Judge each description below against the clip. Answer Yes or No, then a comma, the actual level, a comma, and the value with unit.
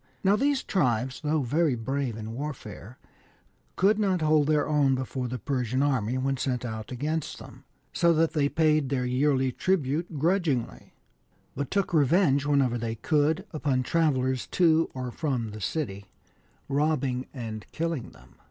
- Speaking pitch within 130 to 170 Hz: Yes, medium, 140 Hz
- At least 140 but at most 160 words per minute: Yes, average, 150 wpm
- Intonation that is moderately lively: Yes, average, 3.9 semitones